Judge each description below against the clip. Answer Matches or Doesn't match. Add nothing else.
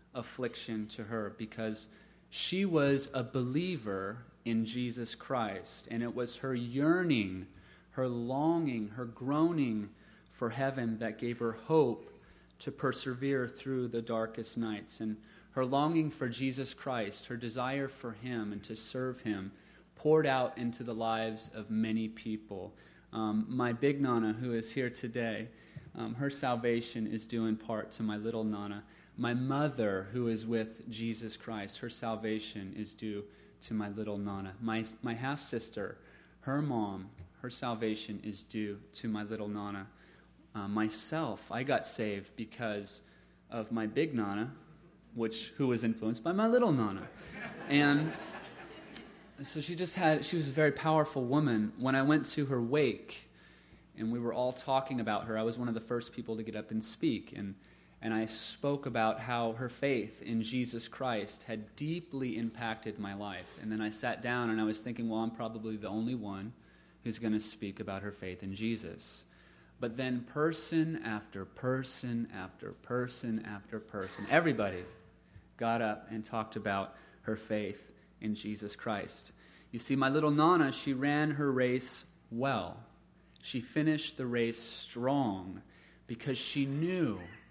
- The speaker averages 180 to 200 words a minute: Doesn't match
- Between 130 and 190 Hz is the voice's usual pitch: Doesn't match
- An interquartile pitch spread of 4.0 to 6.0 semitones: Doesn't match